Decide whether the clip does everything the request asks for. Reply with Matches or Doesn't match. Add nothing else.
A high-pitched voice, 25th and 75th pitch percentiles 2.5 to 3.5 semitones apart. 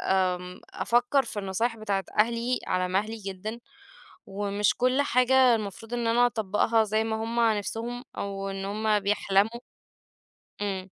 Matches